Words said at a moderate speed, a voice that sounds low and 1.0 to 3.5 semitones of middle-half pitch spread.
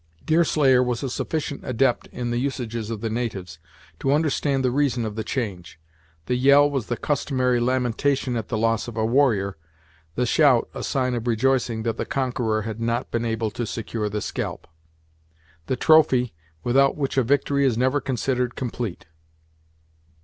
Yes: average, 170 wpm; low, 125 Hz; average, 3.1 semitones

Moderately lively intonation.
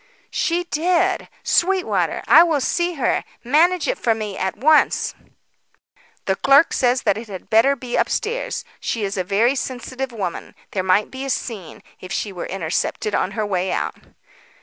No: wide, 7.4 semitones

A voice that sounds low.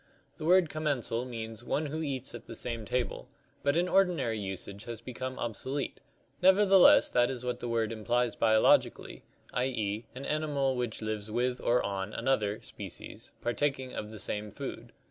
Yes: low, 125 Hz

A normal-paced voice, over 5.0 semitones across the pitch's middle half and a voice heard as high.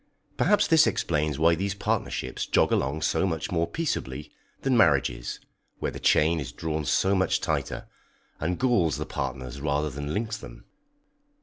No: average, 160 wpm; wide, 5.4 semitones; very low, 80 Hz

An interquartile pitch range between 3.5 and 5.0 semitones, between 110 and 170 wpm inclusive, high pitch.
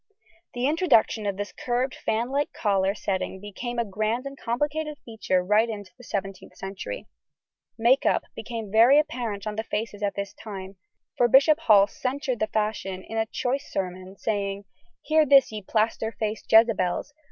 Yes: average, 3.9 semitones; average, 165 wpm; high, 220 Hz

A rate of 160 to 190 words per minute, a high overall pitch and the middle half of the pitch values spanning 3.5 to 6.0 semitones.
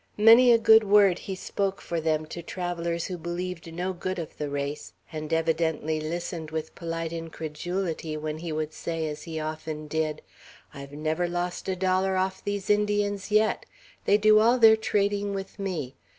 No: average, 175 wpm; medium, 175 Hz; average, 3.8 semitones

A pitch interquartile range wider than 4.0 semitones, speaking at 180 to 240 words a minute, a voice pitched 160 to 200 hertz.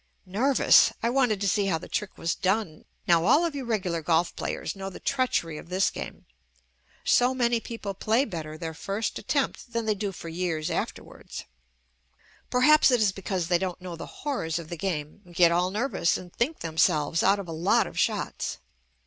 Yes: wide, 5.6 semitones; average, 200 wpm; high, 190 Hz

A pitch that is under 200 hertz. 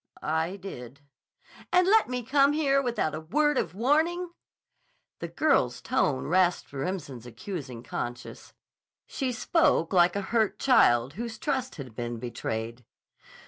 Yes: medium, 185 Hz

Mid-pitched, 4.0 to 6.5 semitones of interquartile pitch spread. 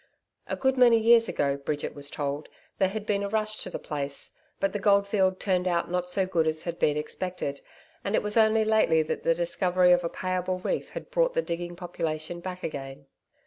Yes: medium, 180 Hz; average, 4.4 semitones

